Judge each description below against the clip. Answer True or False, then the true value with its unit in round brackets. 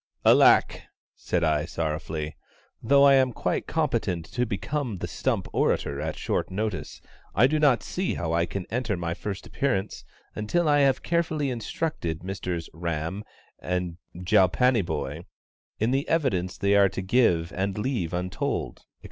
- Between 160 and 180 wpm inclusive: False (150 wpm)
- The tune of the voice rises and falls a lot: True (7.3 semitones)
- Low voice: True (100 Hz)